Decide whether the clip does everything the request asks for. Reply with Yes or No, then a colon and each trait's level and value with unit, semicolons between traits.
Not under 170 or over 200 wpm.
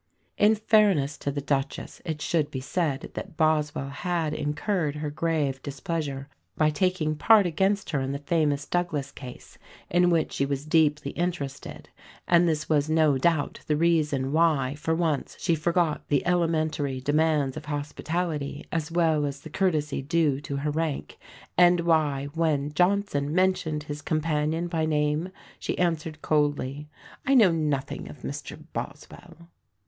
No: average, 155 wpm